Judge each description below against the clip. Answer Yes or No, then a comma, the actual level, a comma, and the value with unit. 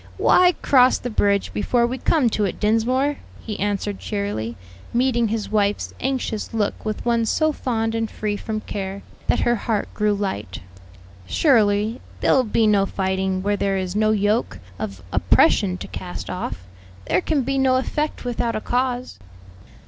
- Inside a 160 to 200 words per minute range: Yes, average, 165 wpm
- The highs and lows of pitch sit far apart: No, average, 3.5 semitones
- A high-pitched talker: Yes, high, 215 Hz